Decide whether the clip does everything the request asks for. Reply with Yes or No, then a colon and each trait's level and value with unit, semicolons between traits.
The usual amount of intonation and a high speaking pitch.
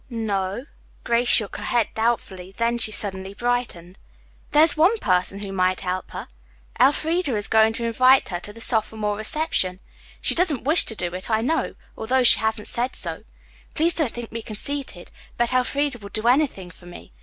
Yes: average, 4.4 semitones; high, 225 Hz